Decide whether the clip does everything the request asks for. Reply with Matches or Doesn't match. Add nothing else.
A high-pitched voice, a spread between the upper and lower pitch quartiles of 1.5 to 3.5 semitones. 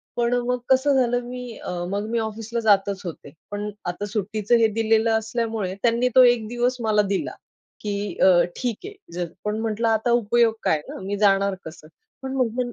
Matches